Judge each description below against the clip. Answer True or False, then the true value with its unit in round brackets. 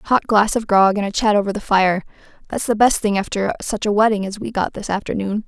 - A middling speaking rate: False (250 wpm)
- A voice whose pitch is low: False (205 Hz)